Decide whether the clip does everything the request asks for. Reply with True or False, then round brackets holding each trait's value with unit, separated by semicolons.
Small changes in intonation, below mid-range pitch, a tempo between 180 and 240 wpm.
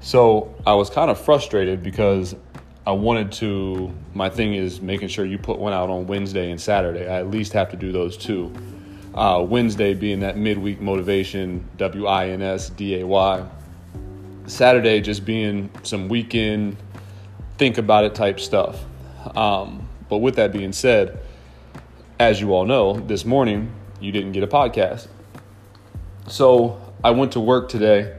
False (2.1 semitones; 100 Hz; 165 wpm)